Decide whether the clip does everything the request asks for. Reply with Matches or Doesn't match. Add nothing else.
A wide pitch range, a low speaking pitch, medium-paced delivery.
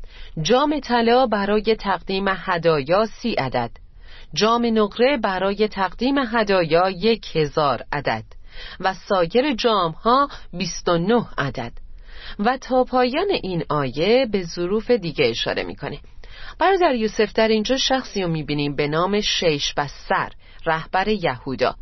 Doesn't match